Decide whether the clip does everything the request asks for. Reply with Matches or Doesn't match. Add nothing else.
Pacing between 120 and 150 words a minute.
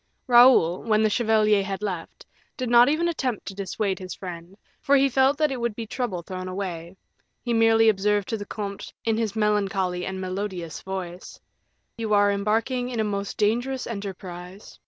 Doesn't match